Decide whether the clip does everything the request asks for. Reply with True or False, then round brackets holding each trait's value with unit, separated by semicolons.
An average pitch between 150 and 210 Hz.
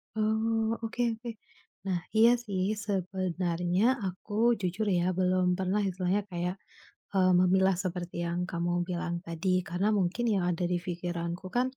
True (185 Hz)